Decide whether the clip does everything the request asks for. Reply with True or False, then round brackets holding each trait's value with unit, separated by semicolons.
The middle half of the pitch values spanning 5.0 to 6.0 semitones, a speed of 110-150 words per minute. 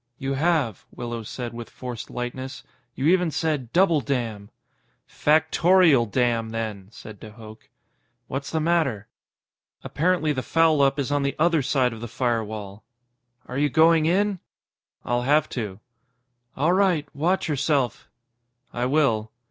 True (5.3 semitones; 140 wpm)